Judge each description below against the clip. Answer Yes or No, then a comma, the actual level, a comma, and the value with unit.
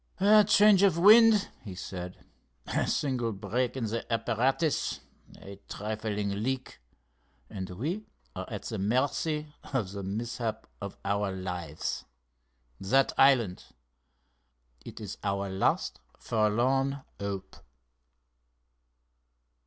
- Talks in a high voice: No, low, 110 Hz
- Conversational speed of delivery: No, slow, 105 wpm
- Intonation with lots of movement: Yes, wide, 5.7 semitones